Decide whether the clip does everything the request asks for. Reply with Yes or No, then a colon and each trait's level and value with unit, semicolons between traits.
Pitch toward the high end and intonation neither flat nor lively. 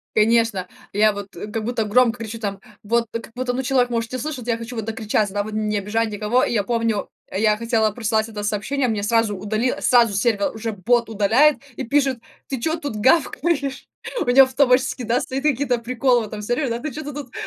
Yes: high, 230 Hz; average, 3.0 semitones